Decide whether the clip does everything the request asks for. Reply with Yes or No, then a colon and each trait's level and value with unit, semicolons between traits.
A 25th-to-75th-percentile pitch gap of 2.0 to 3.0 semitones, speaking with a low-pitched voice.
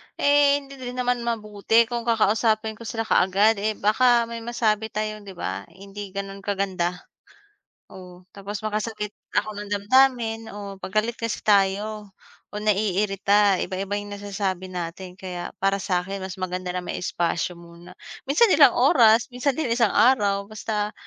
No: average, 2.7 semitones; high, 205 Hz